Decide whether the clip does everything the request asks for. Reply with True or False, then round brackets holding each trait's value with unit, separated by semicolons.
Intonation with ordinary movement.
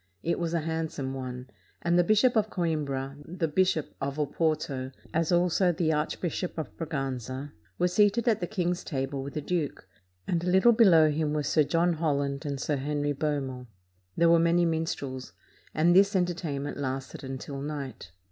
True (3.8 semitones)